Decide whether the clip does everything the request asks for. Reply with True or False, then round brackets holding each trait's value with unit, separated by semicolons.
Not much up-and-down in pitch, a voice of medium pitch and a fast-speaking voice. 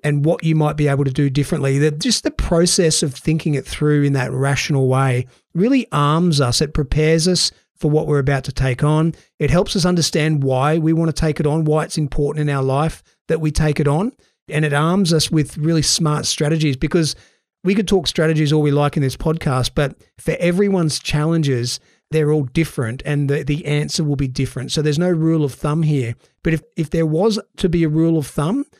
True (2.3 semitones; 155 Hz; 220 wpm)